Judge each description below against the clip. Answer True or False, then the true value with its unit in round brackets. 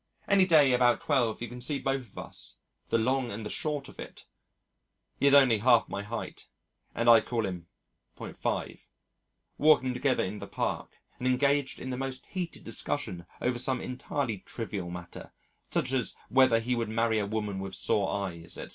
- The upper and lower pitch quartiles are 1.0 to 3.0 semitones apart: False (4.0 semitones)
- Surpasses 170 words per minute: True (180 wpm)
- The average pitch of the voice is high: False (120 Hz)